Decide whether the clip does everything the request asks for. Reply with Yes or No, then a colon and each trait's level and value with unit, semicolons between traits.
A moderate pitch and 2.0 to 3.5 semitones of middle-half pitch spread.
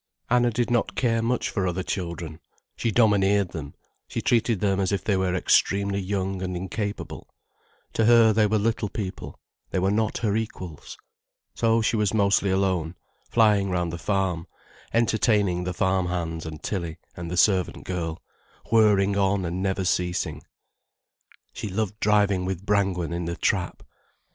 No: very low, 95 Hz; average, 2.9 semitones